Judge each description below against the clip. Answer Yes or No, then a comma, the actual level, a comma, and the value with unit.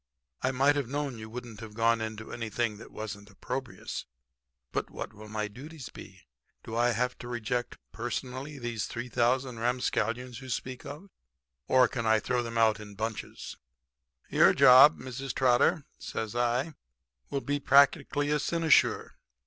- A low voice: Yes, low, 120 Hz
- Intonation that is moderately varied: Yes, average, 3.0 semitones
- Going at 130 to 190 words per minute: Yes, average, 155 wpm